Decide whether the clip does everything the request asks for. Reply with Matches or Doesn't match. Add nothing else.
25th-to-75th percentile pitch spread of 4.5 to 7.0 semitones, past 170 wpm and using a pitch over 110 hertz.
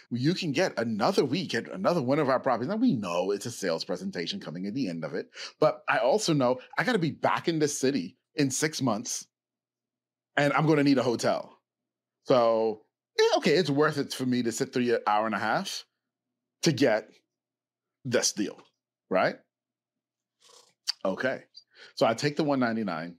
Matches